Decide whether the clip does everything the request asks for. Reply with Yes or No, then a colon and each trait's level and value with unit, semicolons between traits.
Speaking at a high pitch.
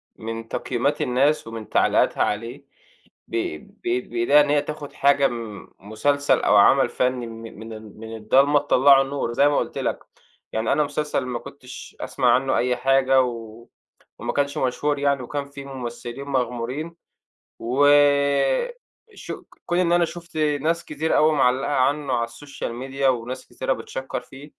No: low, 135 Hz